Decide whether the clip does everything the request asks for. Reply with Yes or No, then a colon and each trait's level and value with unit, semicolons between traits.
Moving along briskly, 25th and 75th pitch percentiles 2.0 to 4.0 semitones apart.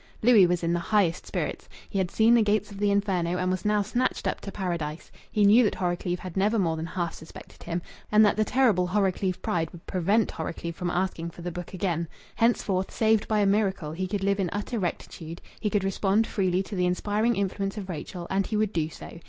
Yes: fast, 225 wpm; average, 3.0 semitones